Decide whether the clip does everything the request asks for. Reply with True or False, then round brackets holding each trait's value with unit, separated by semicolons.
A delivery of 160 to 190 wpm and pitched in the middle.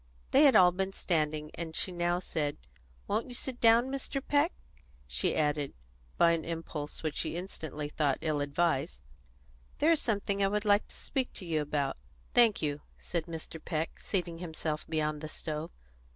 True (175 wpm; 165 Hz)